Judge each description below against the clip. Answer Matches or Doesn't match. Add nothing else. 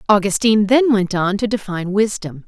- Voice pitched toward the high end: Matches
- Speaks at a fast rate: Doesn't match